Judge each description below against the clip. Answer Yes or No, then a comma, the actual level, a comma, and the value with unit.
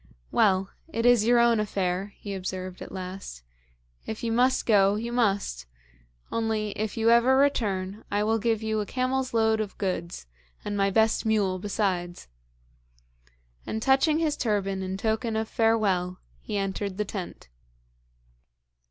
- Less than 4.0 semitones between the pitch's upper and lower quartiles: Yes, average, 3.0 semitones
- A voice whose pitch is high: Yes, high, 210 Hz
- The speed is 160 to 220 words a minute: No, average, 150 wpm